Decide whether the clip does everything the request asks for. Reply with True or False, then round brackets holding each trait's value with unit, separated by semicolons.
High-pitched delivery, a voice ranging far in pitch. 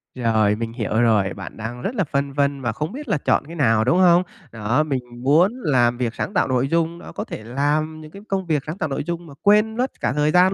False (145 Hz; 6.2 semitones)